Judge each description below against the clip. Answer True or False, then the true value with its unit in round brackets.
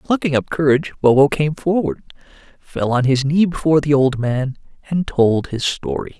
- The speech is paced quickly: False (175 wpm)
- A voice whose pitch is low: False (145 Hz)